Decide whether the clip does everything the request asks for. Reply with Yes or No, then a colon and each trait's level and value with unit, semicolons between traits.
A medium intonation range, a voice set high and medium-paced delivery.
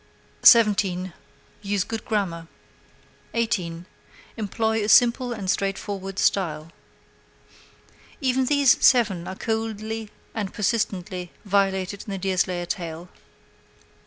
No: average, 3.3 semitones; high, 200 Hz; slow, 100 wpm